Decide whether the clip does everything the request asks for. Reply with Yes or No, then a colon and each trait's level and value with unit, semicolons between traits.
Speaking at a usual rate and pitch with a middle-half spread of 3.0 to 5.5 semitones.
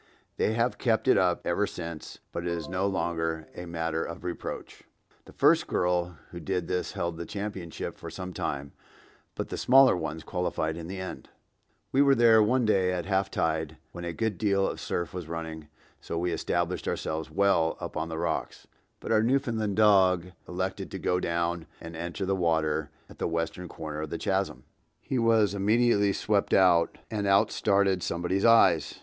Yes: average, 185 wpm; average, 3.4 semitones